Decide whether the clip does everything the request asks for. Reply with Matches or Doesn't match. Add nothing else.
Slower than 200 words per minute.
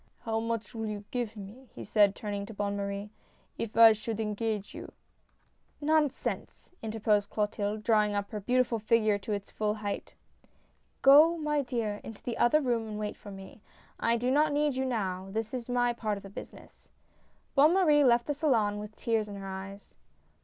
Doesn't match